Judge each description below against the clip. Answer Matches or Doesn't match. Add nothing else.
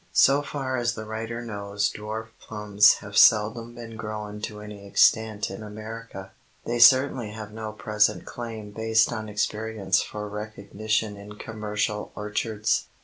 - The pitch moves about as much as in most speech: Doesn't match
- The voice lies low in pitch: Matches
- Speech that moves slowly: Doesn't match